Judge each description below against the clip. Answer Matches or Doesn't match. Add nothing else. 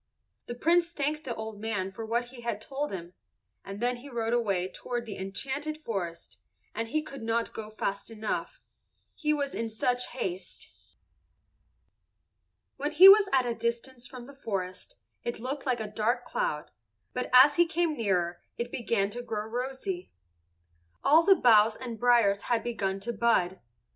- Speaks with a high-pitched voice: Matches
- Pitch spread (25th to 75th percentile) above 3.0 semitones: Matches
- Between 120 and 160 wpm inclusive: Doesn't match